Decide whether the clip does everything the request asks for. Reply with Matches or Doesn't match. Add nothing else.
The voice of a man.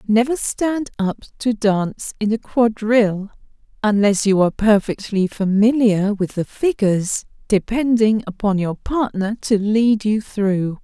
Doesn't match